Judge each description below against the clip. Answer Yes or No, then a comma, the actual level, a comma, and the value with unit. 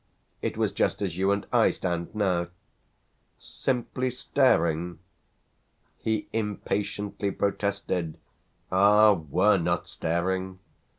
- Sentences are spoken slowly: Yes, slow, 100 wpm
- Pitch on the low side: Yes, low, 100 Hz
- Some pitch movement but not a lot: Yes, average, 3.2 semitones